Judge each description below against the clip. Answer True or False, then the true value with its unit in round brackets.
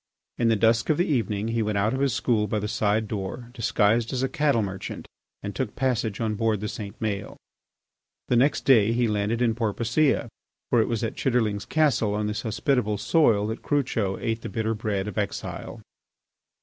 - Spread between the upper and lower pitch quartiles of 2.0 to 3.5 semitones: True (2.6 semitones)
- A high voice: False (110 Hz)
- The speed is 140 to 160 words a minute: False (195 wpm)